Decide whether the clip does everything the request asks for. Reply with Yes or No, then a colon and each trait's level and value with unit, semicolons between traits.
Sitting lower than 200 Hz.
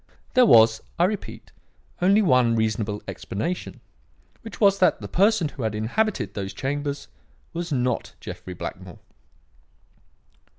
Yes: medium, 140 Hz